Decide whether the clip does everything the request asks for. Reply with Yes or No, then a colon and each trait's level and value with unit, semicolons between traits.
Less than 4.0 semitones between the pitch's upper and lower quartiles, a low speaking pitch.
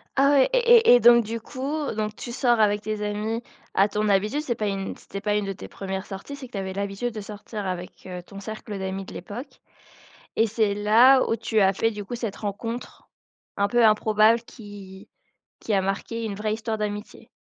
No: narrow, 2.5 semitones; high, 215 Hz